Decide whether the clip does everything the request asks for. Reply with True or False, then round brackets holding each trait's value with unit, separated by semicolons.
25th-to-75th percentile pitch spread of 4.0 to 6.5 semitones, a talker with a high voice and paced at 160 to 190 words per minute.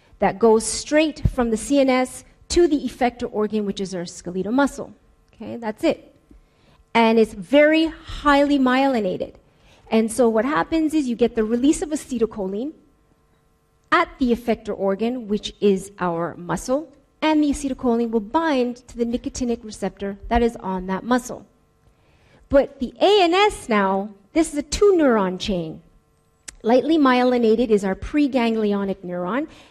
False (5.2 semitones; 235 Hz; 145 wpm)